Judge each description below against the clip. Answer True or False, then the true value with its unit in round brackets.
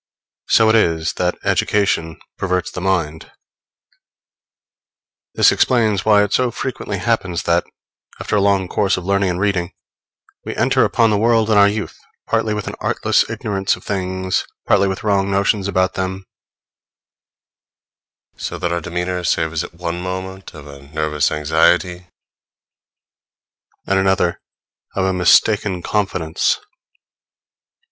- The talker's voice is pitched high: False (95 Hz)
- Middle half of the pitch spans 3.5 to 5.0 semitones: False (2.7 semitones)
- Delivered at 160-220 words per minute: False (135 wpm)